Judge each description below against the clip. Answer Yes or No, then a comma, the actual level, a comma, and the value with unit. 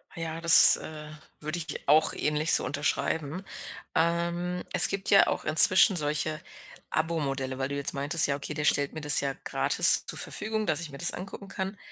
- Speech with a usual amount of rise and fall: Yes, average, 3.0 semitones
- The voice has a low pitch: No, medium, 155 Hz